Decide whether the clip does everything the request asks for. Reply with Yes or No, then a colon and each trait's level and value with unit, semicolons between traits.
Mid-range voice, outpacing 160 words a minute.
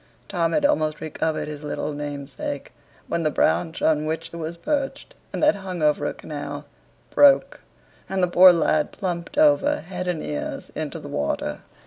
Yes: medium, 165 Hz; average, 170 wpm